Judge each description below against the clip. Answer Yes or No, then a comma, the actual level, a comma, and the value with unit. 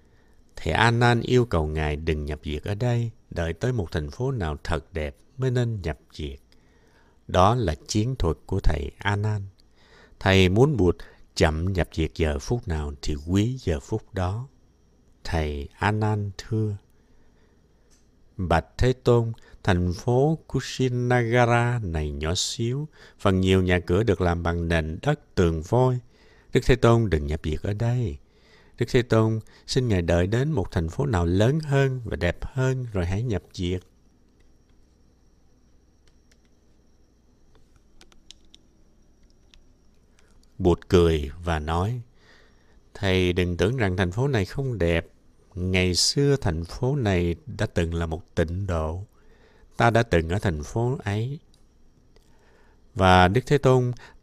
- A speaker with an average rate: No, slow, 145 wpm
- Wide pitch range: Yes, wide, 6.3 semitones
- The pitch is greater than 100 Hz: No, very low, 95 Hz